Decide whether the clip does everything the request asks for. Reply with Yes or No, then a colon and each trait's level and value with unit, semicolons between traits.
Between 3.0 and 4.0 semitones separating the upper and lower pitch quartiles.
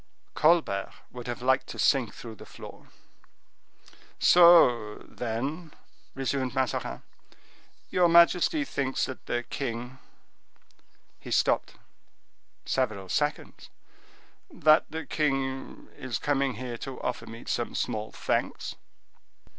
No: average, 4.7 semitones